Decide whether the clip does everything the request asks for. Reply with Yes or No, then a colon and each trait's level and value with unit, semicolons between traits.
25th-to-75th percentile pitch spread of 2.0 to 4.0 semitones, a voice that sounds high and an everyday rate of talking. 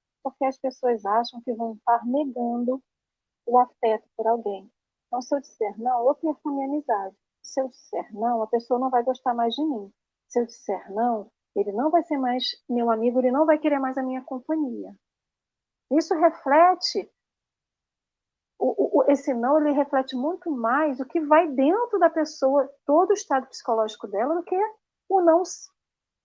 No: average, 4.4 semitones; very high, 265 Hz; average, 175 wpm